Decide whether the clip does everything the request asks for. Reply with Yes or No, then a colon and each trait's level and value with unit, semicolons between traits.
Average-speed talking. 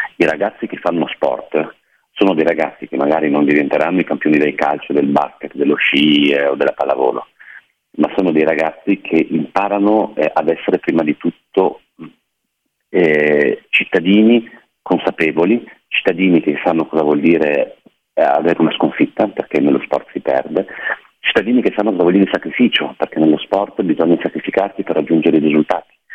Yes: average, 160 wpm